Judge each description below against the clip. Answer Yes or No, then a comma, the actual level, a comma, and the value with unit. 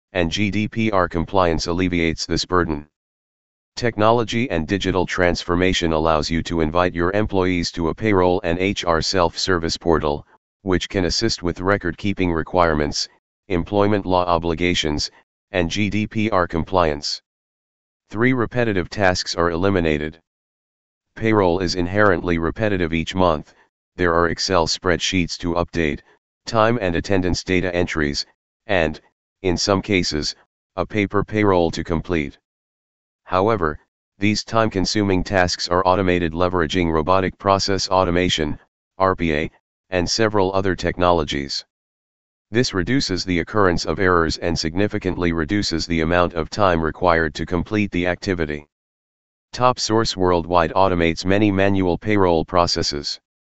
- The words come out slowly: Yes, slow, 120 wpm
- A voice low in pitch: Yes, very low, 90 Hz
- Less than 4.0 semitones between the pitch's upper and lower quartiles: Yes, average, 2.9 semitones